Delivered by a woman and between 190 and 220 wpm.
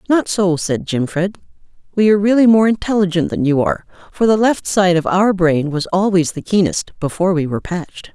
Yes: female; average, 200 wpm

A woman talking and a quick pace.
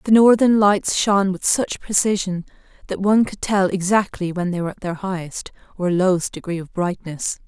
No: female; average, 185 wpm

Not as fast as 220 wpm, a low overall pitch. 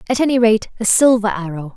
No: fast, 205 wpm; high, 220 Hz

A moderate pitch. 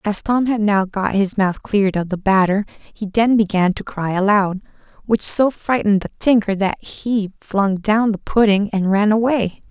No: high, 205 Hz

